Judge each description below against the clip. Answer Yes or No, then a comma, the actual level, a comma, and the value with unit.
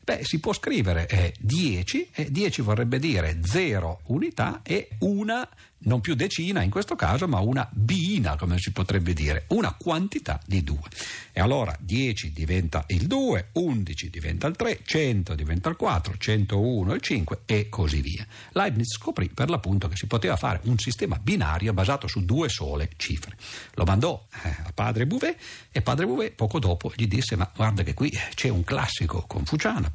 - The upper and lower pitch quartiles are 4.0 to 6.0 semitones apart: Yes, wide, 5.5 semitones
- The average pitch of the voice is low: Yes, low, 100 Hz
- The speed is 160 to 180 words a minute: Yes, fast, 170 wpm